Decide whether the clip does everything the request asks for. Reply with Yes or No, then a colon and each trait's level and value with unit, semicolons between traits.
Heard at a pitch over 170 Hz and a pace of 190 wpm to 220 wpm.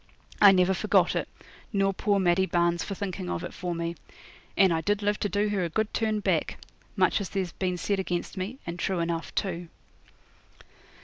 Yes: high, 190 Hz; average, 195 wpm